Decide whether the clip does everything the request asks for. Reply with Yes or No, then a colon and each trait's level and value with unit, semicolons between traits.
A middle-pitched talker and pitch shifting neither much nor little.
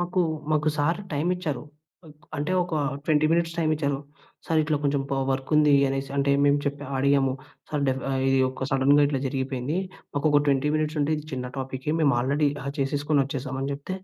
No: medium, 145 Hz; narrow, 2.0 semitones